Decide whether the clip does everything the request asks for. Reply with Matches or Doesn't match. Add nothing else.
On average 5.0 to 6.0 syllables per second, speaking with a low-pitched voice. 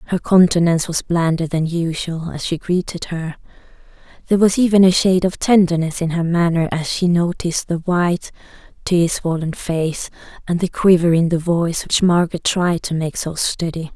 Doesn't match